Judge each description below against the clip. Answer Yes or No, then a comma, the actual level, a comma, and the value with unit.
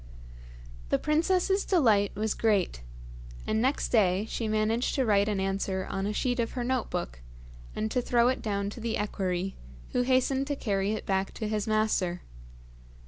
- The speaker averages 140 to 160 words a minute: No, average, 175 wpm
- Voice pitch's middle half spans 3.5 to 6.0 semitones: Yes, average, 3.8 semitones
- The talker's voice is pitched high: Yes, high, 215 Hz